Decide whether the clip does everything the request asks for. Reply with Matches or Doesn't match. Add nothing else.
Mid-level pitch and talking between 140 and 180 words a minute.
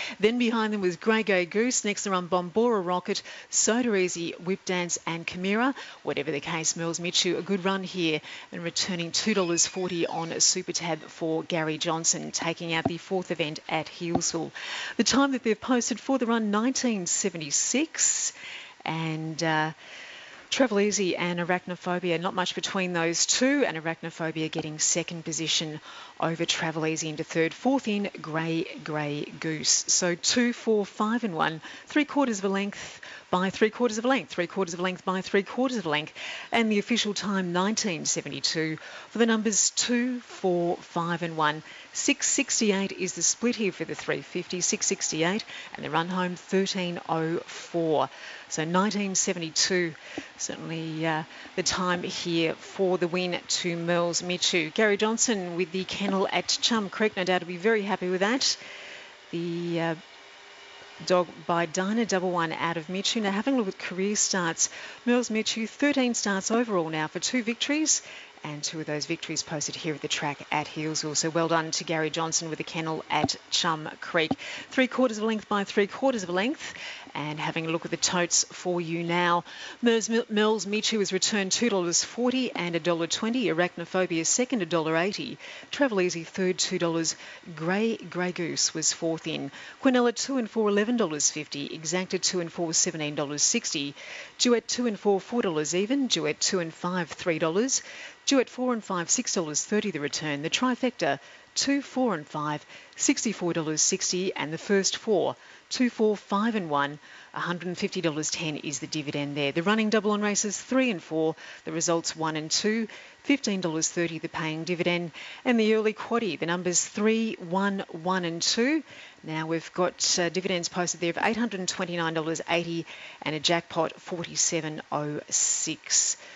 Matches